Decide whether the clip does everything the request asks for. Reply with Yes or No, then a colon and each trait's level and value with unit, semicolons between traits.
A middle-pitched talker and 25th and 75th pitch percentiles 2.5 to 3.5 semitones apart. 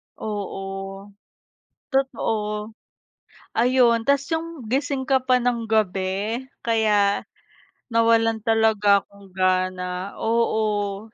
No: high, 220 Hz; average, 2.8 semitones